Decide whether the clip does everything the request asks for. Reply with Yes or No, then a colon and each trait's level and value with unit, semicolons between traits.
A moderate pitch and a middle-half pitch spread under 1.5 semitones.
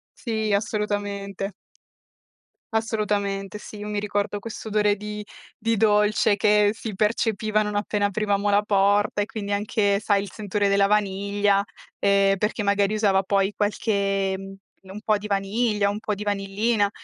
No: high, 205 Hz; narrow, 1.0 semitones